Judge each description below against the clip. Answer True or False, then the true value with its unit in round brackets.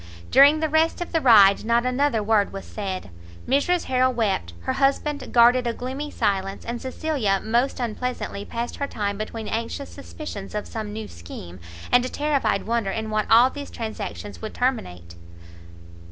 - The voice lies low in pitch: False (235 Hz)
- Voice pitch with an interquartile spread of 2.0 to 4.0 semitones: False (4.5 semitones)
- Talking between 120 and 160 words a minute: False (170 wpm)